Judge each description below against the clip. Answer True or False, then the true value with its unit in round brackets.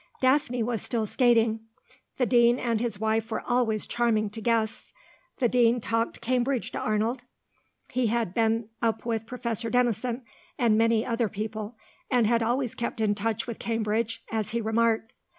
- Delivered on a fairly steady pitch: True (1.5 semitones)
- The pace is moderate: True (165 wpm)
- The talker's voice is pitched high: True (230 Hz)